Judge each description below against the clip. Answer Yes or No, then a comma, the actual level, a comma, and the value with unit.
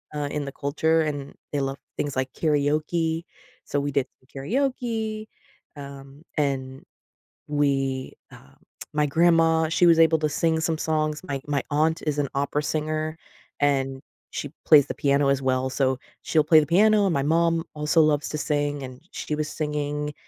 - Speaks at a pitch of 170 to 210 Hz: No, medium, 150 Hz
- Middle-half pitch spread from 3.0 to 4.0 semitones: No, narrow, 2.4 semitones